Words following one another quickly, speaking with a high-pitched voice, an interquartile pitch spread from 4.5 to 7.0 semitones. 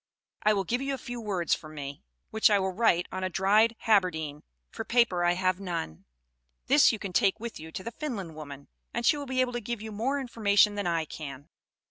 Yes: fast, 225 wpm; high, 200 Hz; wide, 5.4 semitones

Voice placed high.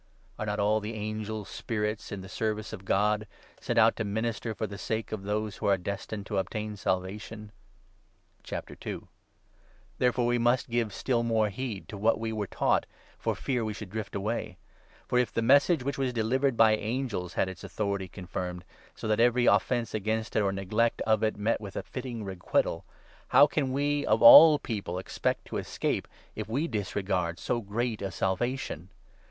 No: low, 110 Hz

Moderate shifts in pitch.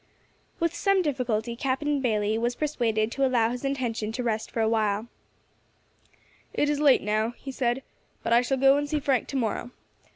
Yes: average, 3.6 semitones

